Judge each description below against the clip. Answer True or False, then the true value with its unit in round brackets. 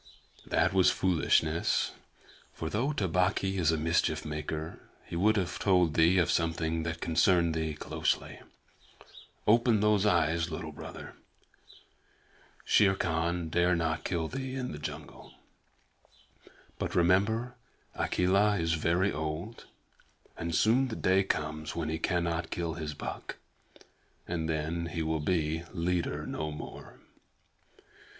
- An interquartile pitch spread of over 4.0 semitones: False (2.9 semitones)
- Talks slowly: True (130 wpm)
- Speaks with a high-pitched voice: False (85 Hz)